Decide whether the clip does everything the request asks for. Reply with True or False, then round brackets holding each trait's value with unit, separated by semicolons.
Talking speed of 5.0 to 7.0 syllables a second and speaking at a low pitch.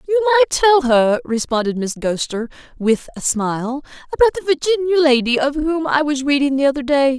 False (6.0 syllables/s; 285 Hz)